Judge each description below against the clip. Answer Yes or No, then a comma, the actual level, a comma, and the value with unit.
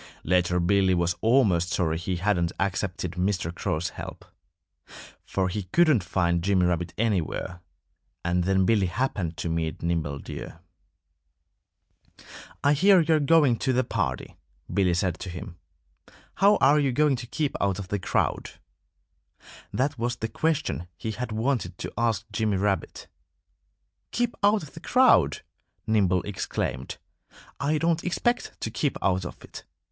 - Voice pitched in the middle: No, low, 100 Hz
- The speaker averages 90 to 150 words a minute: Yes, average, 145 wpm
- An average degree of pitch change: No, wide, 7.2 semitones